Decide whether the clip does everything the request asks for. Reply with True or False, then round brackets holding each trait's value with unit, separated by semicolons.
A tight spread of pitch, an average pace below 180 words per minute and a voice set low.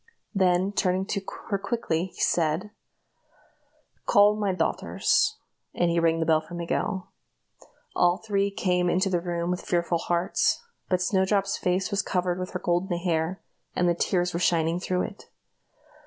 False (1.9 semitones; 155 wpm; 180 Hz)